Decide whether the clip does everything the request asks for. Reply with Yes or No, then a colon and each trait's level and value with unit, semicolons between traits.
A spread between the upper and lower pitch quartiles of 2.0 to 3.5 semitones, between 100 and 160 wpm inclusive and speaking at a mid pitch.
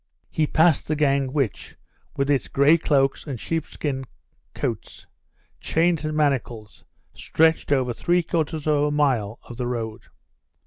Yes: average, 3.2 semitones; average, 140 wpm; medium, 145 Hz